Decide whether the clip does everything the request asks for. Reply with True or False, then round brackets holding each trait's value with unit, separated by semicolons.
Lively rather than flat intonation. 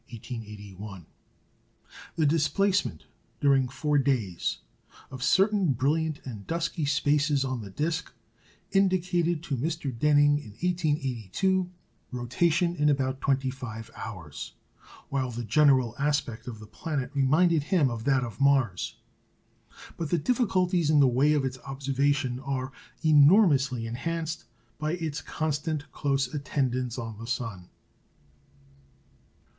False (4.0 semitones)